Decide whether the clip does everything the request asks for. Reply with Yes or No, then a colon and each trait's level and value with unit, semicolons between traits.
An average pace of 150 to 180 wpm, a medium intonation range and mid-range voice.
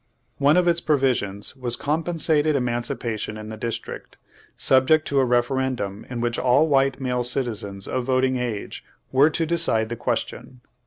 No: average, 160 wpm; average, 3.0 semitones; low, 125 Hz